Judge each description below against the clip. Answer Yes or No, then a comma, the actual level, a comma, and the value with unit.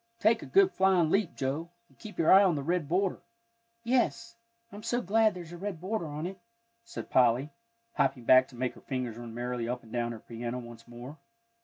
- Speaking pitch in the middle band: Yes, medium, 160 Hz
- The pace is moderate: No, fast, 210 wpm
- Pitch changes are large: Yes, wide, 8.3 semitones